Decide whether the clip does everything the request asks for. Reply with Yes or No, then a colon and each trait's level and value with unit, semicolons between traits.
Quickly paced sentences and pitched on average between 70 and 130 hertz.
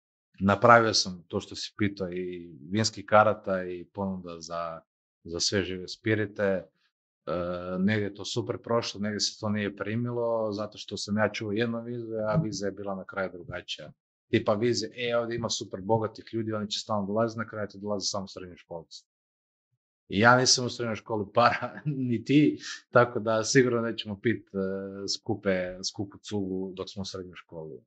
Yes: fast, 170 wpm; low, 105 Hz